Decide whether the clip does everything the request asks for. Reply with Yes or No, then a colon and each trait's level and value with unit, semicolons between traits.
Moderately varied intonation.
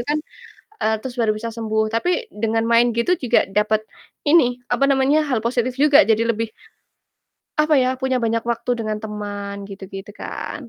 Yes: average, 3.1 semitones